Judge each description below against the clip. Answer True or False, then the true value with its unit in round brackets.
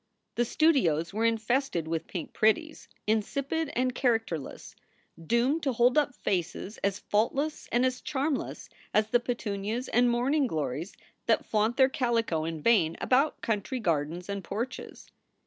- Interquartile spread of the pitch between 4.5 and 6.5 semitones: True (4.9 semitones)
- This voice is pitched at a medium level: False (230 Hz)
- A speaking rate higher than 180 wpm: False (145 wpm)